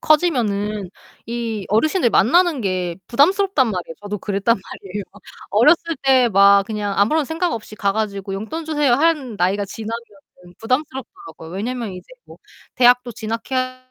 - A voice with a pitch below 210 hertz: No, high, 225 Hz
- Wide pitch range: No, average, 4.9 semitones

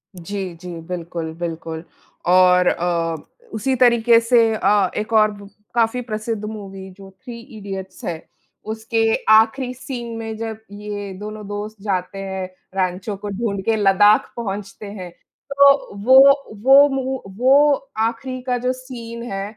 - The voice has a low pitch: No, high, 210 Hz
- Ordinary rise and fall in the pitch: Yes, average, 3.5 semitones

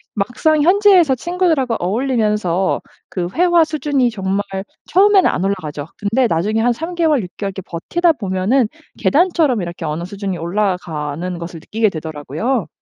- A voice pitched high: Yes, high, 215 Hz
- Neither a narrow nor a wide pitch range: No, wide, 8.8 semitones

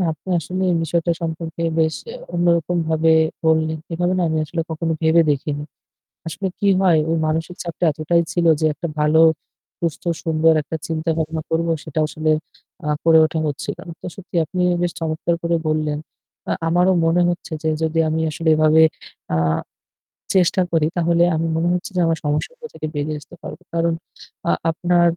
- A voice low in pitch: No, medium, 165 Hz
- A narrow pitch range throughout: Yes, narrow, 1.6 semitones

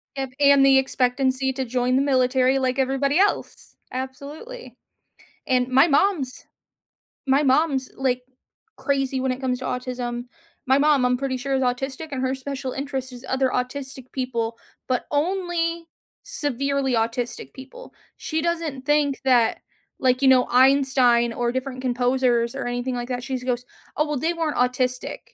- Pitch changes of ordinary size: No, narrow, 1.8 semitones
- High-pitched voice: Yes, very high, 265 Hz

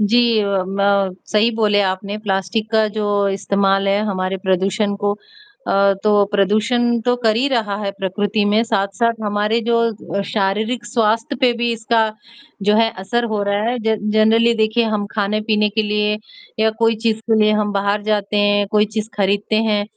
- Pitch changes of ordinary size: No, narrow, 1.8 semitones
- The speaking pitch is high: Yes, high, 210 Hz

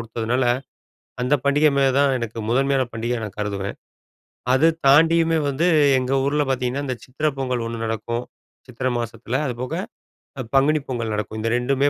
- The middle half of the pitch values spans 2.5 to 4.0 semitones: Yes, average, 3.2 semitones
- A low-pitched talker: Yes, low, 125 Hz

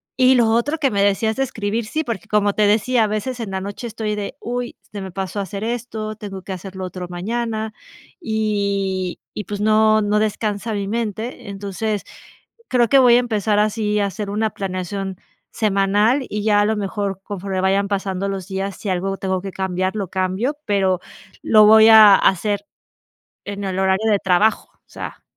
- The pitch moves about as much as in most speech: No, narrow, 2.1 semitones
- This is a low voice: No, high, 205 Hz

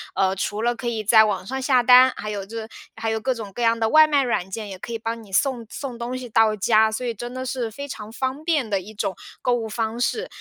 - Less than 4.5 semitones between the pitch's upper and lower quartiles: Yes, average, 2.9 semitones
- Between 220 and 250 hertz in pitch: Yes, high, 230 Hz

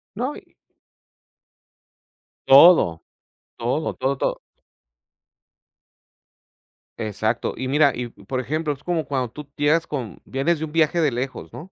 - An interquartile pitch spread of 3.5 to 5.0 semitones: Yes, average, 3.8 semitones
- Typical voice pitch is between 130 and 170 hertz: Yes, medium, 140 Hz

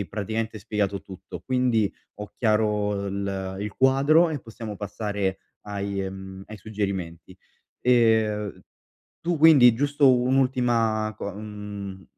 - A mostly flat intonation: No, average, 3.6 semitones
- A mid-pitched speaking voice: No, low, 105 Hz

